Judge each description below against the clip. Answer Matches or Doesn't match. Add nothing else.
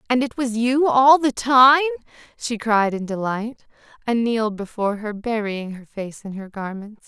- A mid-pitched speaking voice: Doesn't match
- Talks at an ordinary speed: Matches